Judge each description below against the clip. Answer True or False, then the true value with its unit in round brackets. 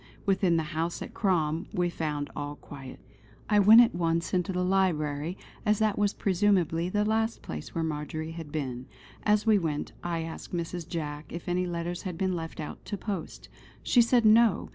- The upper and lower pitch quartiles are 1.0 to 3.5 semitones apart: False (4.0 semitones)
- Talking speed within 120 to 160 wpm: False (185 wpm)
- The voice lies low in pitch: False (175 Hz)